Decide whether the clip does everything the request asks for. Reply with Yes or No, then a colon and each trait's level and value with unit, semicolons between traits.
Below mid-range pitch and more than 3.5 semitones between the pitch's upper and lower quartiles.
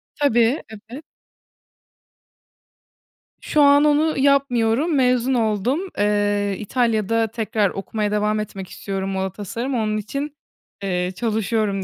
No: high, 225 Hz; average, 4.3 semitones